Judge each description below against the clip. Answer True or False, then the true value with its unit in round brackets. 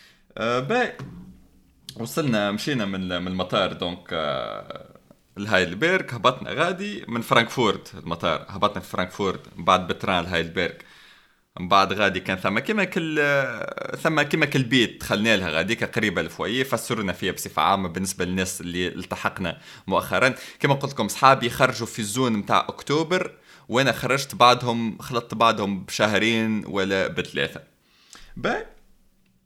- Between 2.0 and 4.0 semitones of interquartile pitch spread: False (5.5 semitones)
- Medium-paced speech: True (120 wpm)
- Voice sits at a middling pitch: False (110 Hz)